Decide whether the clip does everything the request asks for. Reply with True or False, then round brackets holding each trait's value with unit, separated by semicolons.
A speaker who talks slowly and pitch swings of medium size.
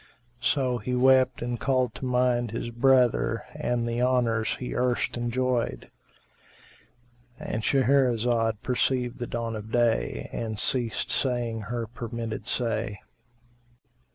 False (115 wpm; 1.6 semitones)